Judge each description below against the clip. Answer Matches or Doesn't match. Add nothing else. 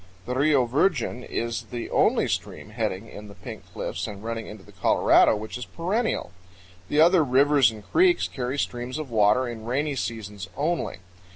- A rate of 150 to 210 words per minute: Matches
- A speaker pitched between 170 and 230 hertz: Doesn't match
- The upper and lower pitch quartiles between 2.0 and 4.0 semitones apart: Doesn't match